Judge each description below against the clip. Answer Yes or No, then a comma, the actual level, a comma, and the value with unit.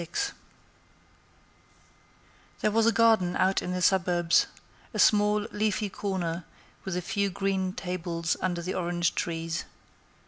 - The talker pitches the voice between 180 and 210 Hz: Yes, medium, 185 Hz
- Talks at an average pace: No, slow, 130 wpm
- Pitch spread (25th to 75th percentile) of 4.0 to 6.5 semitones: No, average, 3.0 semitones